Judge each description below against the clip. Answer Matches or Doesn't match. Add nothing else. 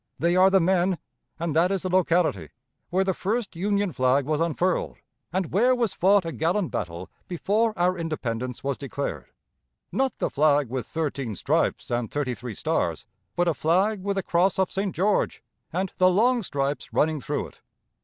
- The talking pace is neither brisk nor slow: Matches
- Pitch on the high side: Doesn't match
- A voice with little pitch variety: Doesn't match